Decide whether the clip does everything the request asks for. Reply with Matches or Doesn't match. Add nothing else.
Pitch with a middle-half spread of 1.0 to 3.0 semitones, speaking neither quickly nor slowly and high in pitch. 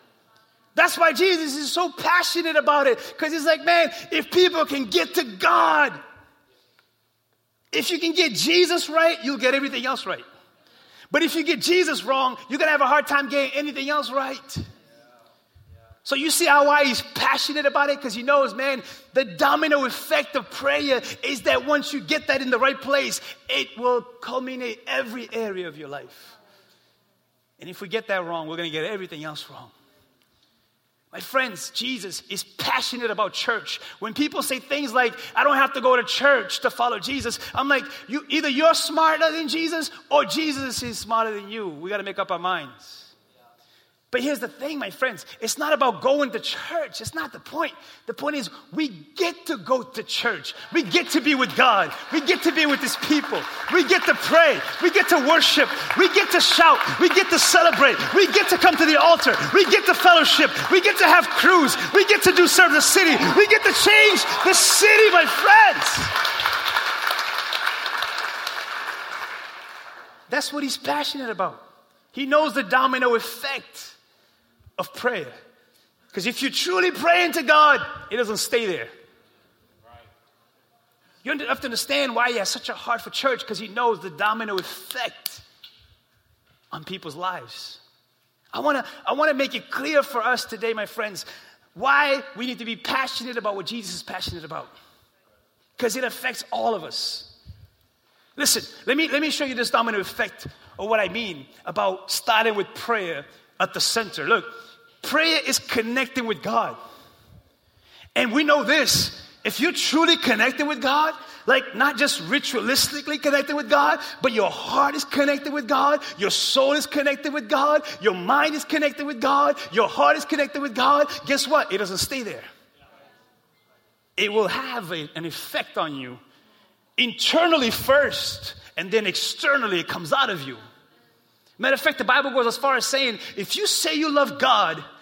Doesn't match